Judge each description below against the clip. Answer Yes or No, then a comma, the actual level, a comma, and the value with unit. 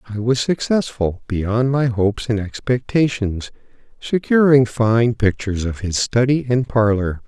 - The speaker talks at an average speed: No, slow, 130 wpm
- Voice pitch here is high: No, low, 115 Hz